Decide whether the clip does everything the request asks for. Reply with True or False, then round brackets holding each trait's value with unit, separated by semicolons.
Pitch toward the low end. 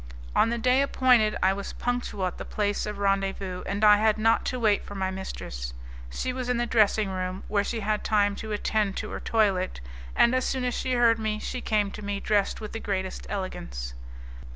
False (210 Hz)